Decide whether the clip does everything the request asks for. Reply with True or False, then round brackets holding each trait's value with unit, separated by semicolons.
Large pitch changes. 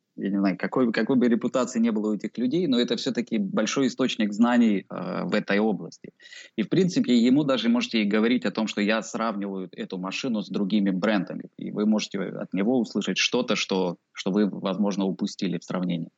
False (3.9 semitones)